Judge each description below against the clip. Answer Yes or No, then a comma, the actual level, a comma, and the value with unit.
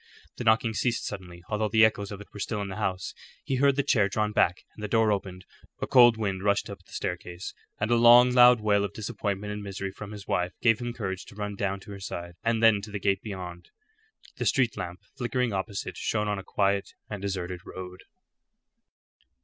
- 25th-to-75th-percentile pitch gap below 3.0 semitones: Yes, narrow, 2.6 semitones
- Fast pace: Yes, fast, 215 wpm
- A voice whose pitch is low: Yes, low, 105 Hz